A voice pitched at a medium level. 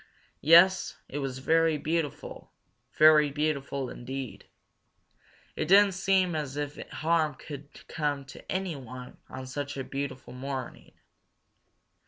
Yes: medium, 145 Hz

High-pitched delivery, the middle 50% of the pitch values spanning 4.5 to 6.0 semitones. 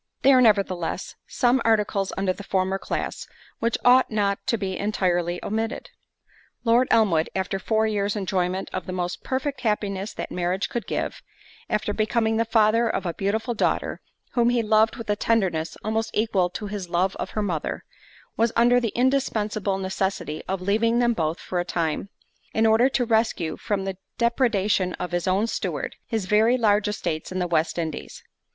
No: high, 210 Hz; average, 3.4 semitones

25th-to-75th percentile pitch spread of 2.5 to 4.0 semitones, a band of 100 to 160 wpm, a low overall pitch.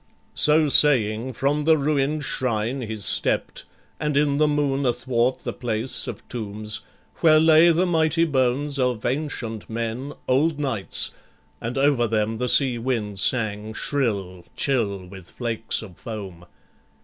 No: average, 4.8 semitones; average, 140 wpm; low, 125 Hz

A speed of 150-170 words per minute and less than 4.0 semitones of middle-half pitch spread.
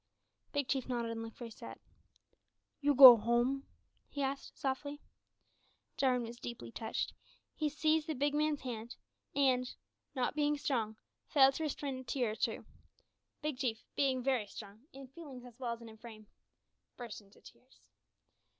Yes: average, 160 wpm; average, 3.3 semitones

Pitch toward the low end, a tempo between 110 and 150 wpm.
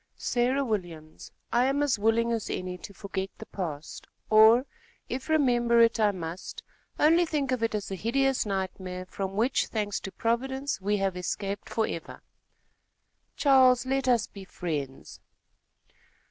No: high, 220 Hz; average, 145 wpm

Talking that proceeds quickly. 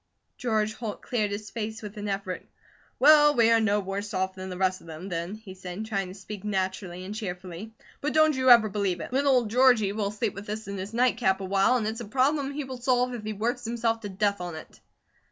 Yes: fast, 240 wpm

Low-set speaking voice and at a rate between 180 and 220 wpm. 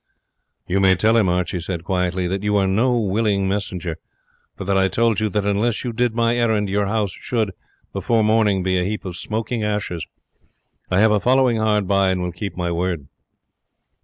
Yes: low, 100 Hz; average, 195 wpm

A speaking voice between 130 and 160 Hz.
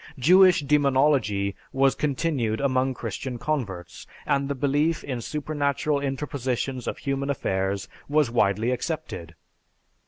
Yes: low, 135 Hz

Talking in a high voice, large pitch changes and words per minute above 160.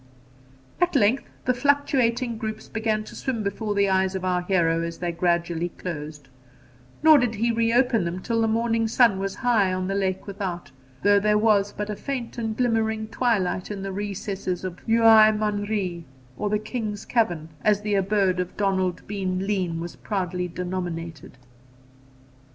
No: high, 205 Hz; average, 3.5 semitones; average, 170 wpm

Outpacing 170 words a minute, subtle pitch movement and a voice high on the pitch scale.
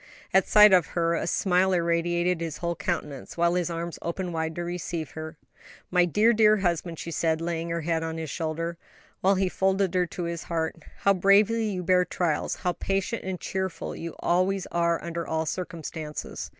No: average, 190 wpm; narrow, 2.1 semitones; medium, 170 Hz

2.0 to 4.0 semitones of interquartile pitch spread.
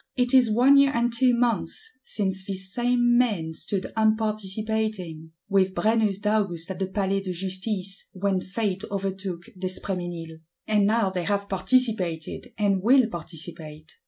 Yes: average, 3.2 semitones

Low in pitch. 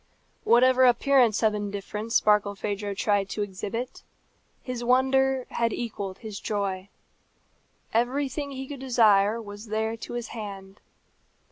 No: high, 220 Hz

